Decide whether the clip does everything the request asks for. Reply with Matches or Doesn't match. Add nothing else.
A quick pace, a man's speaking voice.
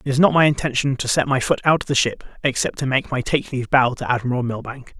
Matches